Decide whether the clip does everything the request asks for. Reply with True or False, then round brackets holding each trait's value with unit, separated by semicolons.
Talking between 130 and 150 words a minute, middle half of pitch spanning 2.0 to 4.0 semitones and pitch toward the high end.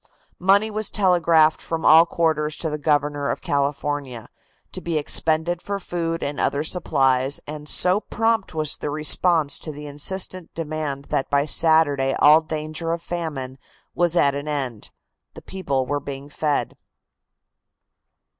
False (145 wpm; 2.9 semitones; 155 Hz)